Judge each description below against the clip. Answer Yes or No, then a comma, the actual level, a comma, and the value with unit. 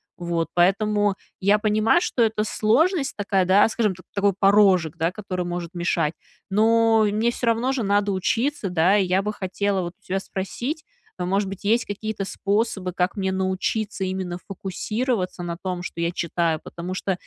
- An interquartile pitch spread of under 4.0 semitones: Yes, average, 2.9 semitones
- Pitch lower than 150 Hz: No, high, 195 Hz